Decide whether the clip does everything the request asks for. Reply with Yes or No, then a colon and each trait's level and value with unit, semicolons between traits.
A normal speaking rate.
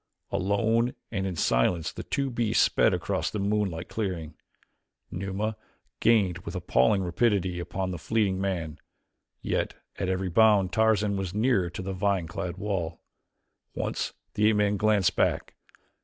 Yes: average, 145 wpm